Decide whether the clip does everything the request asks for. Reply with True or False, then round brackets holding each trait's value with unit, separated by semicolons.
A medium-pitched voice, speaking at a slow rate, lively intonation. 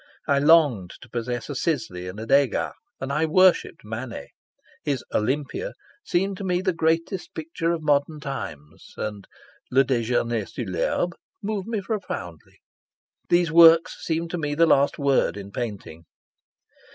True (145 Hz; 130 wpm; 6.3 semitones)